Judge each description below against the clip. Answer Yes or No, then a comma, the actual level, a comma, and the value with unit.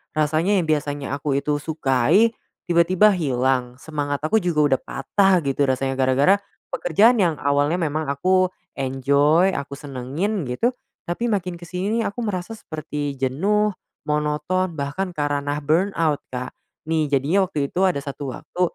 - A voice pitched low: No, medium, 150 Hz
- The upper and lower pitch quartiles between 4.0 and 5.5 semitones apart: Yes, average, 4.6 semitones